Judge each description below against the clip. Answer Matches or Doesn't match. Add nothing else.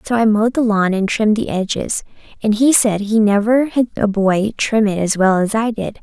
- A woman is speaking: Matches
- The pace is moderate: Doesn't match